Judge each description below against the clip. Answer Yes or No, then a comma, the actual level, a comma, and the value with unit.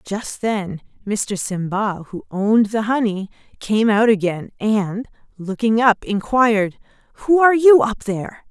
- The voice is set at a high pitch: Yes, high, 215 Hz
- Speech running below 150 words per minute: Yes, average, 140 wpm